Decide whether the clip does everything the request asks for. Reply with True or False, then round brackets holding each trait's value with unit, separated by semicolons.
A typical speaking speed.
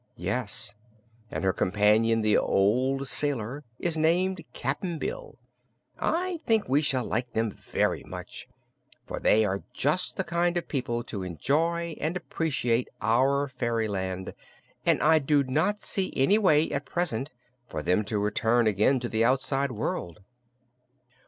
True (145 wpm)